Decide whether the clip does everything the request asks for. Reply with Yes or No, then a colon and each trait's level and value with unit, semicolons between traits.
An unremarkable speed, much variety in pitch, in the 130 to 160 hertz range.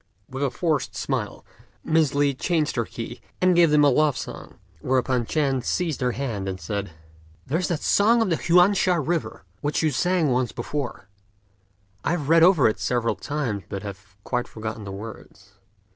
Yes: average, 180 wpm; wide, 6.0 semitones; medium, 140 Hz